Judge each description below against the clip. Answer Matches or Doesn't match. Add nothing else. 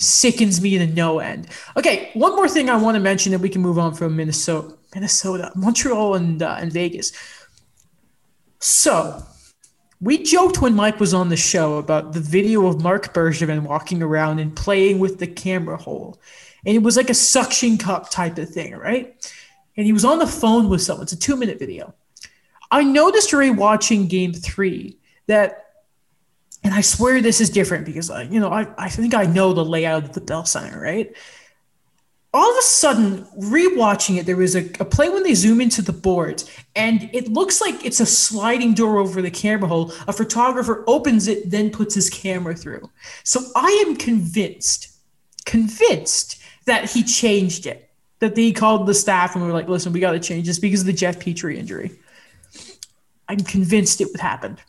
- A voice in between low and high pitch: Doesn't match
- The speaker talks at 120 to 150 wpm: Doesn't match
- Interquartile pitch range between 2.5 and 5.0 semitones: Matches